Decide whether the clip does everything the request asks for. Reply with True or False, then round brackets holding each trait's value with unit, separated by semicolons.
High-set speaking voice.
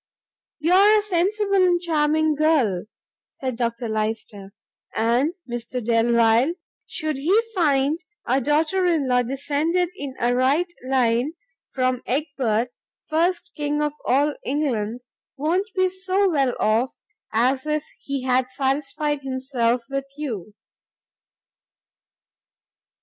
True (275 Hz)